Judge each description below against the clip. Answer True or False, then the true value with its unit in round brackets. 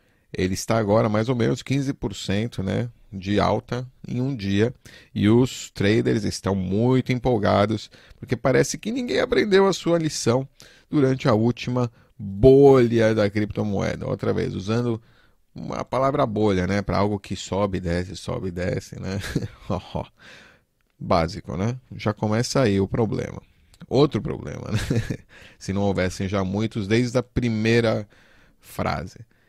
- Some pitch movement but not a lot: True (3.8 semitones)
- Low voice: True (115 Hz)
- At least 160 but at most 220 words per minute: False (140 wpm)